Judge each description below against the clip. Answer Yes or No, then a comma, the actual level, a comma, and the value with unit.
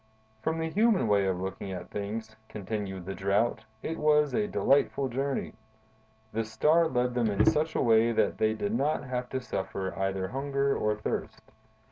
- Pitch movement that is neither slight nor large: No, wide, 5.7 semitones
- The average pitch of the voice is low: Yes, low, 115 Hz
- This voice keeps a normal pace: Yes, average, 175 wpm